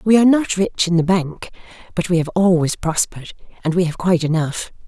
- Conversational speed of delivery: No, fast, 210 wpm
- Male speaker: No, female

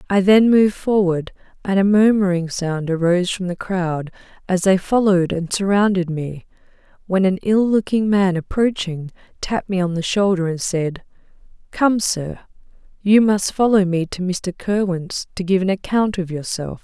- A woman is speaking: Yes, female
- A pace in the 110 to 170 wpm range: Yes, average, 165 wpm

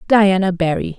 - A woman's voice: Yes, female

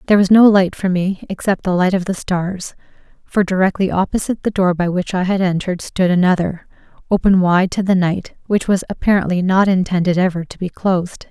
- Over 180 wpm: Yes, average, 200 wpm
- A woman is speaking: Yes, female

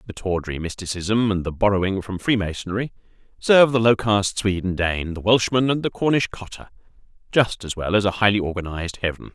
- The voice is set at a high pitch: No, low, 100 Hz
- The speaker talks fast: No, average, 185 wpm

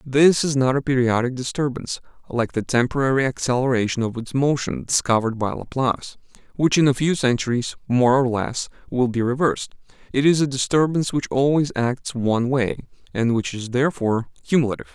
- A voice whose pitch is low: Yes, low, 130 Hz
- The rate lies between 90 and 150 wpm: No, average, 165 wpm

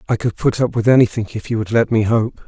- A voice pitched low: Yes, low, 115 Hz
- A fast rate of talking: Yes, fast, 290 wpm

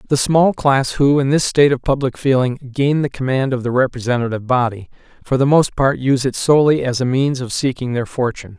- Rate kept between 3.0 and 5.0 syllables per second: No, 5.9 syllables/s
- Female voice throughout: No, male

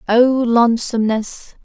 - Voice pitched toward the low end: No, high, 235 Hz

